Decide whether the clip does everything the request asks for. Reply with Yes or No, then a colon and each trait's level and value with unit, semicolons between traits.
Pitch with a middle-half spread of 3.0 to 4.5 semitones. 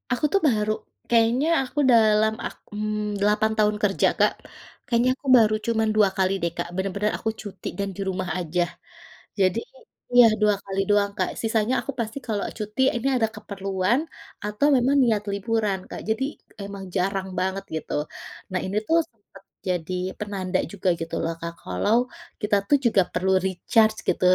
No: narrow, 2.6 semitones